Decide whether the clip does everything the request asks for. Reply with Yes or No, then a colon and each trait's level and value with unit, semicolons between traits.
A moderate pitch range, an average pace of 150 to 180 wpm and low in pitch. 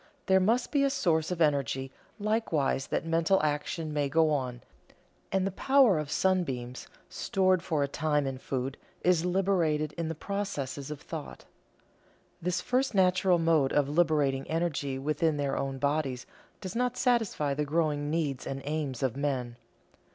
No: average, 4.8 semitones; average, 160 wpm; medium, 155 Hz